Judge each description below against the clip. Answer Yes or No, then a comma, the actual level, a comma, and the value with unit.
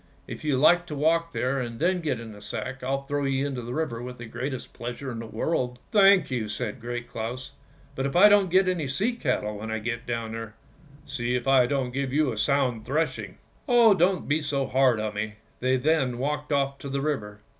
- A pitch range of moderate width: Yes, average, 4.0 semitones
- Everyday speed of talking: No, fast, 235 wpm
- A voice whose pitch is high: No, low, 130 Hz